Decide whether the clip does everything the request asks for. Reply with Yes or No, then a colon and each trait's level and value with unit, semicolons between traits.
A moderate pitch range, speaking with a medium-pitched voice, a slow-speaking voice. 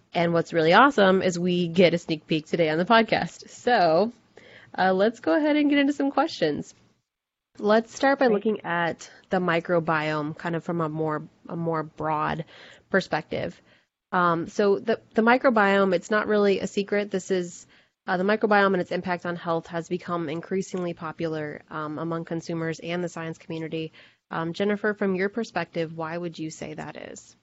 No: average, 3.7 semitones; medium, 175 Hz; average, 180 wpm